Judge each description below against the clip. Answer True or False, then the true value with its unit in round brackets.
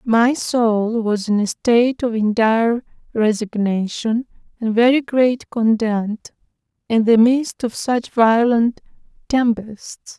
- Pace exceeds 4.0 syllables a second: False (3.4 syllables/s)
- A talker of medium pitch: False (230 Hz)